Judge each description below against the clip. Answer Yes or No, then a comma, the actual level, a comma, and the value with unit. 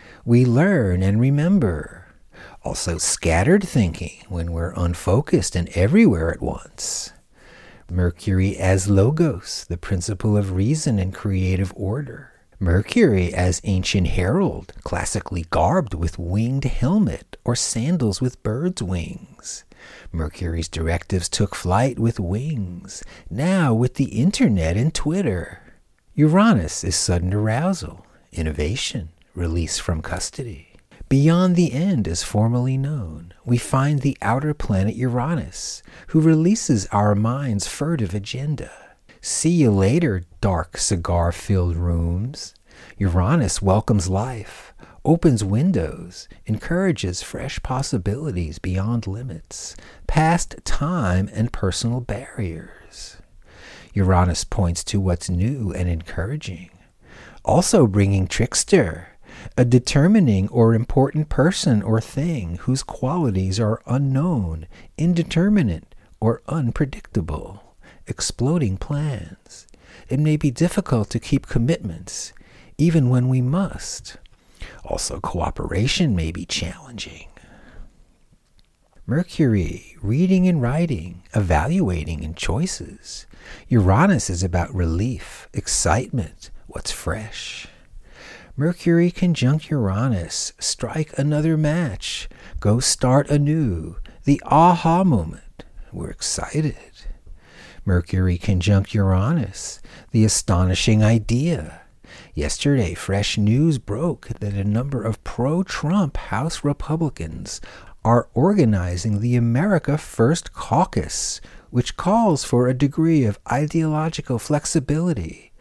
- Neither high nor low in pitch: No, low, 115 Hz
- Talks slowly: Yes, slow, 105 wpm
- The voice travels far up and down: Yes, wide, 7.9 semitones